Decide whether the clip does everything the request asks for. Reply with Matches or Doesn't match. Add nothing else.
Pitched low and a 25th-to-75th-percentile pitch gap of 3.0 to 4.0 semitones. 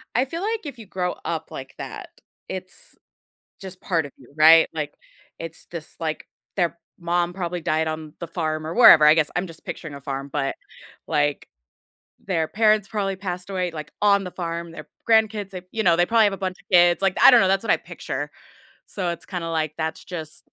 Doesn't match